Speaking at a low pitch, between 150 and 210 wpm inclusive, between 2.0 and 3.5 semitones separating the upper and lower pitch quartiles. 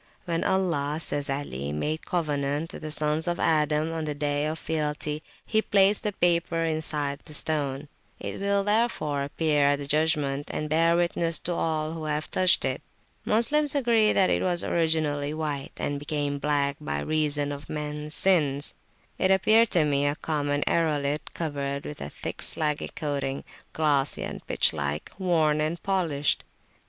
No: medium, 155 Hz; average, 165 wpm; average, 2.7 semitones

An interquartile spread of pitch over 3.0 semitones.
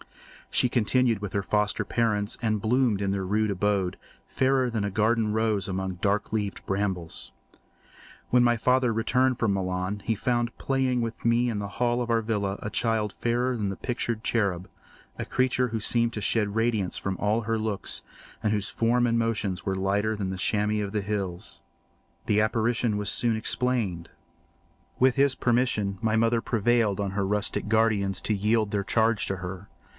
No: average, 2.7 semitones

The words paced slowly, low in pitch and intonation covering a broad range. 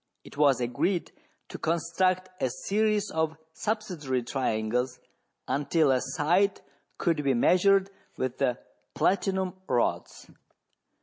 No: slow, 110 wpm; medium, 160 Hz; wide, 6.4 semitones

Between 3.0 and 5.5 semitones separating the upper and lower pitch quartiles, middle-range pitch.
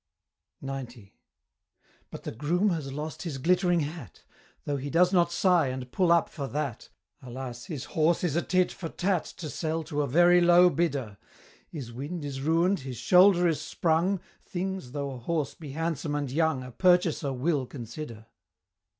Yes: average, 4.4 semitones; medium, 155 Hz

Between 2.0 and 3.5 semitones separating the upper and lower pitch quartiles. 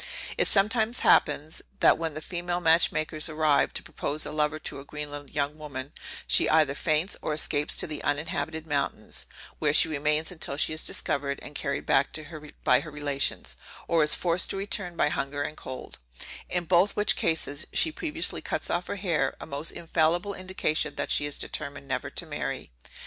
Yes: average, 3.0 semitones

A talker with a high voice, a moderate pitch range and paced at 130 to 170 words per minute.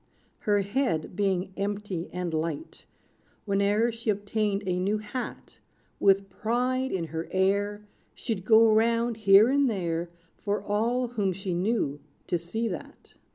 Yes: high, 205 Hz; average, 3.2 semitones; average, 140 wpm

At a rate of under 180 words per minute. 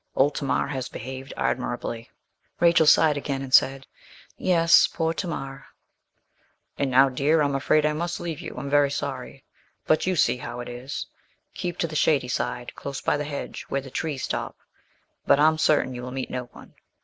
No: average, 185 wpm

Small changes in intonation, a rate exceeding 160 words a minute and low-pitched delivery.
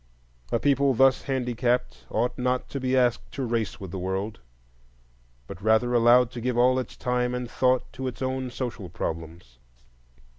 Yes: narrow, 2.3 semitones; average, 170 wpm; low, 125 Hz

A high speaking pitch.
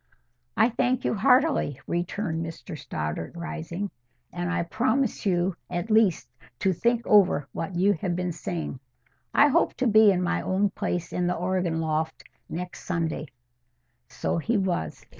No: medium, 180 Hz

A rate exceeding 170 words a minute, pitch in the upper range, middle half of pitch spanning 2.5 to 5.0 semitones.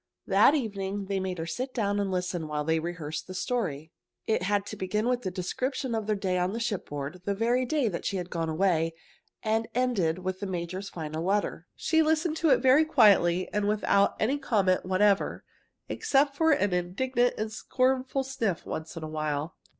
No: average, 195 wpm; high, 200 Hz; wide, 5.6 semitones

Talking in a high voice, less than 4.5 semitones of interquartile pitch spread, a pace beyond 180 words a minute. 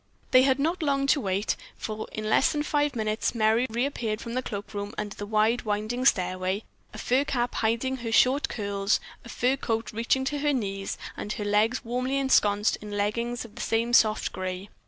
Yes: high, 225 Hz; average, 3.7 semitones; average, 195 wpm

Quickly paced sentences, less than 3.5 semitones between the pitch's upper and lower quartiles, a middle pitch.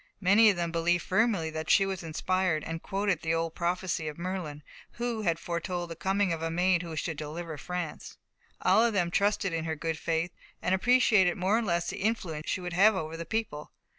Yes: fast, 210 wpm; average, 2.9 semitones; medium, 175 Hz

